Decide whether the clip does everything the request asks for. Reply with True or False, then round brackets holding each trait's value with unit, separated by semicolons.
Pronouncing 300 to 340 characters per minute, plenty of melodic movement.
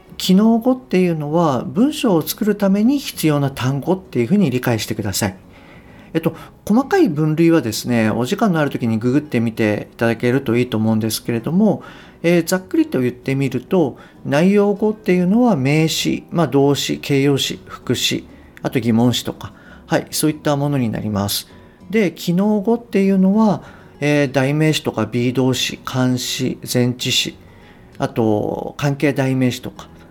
True (335 characters per minute; 7.4 semitones)